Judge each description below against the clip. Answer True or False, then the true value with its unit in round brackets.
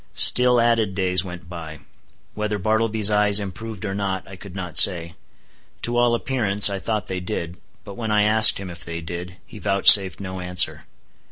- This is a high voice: False (100 Hz)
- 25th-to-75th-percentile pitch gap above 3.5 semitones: False (3.0 semitones)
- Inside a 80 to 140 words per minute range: False (180 wpm)